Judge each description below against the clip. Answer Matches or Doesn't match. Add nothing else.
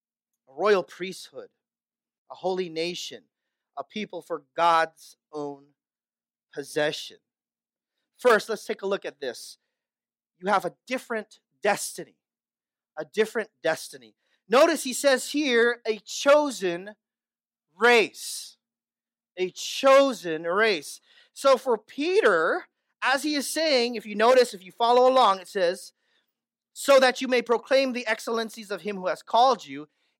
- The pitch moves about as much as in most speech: Doesn't match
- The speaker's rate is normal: Doesn't match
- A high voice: Matches